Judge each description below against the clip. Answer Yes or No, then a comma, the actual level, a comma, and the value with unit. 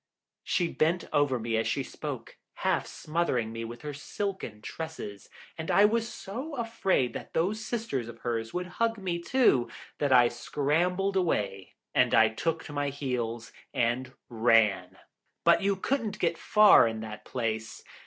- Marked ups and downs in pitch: Yes, wide, 8.7 semitones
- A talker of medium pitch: Yes, medium, 145 Hz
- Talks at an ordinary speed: Yes, average, 160 wpm